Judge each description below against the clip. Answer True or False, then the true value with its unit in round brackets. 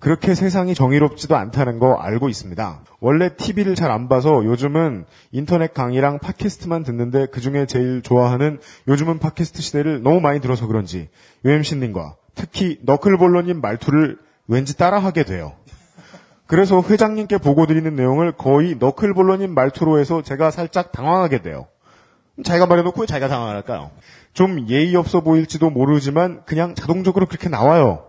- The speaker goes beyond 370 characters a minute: True (380 characters per minute)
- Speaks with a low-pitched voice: False (155 Hz)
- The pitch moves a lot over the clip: False (5.0 semitones)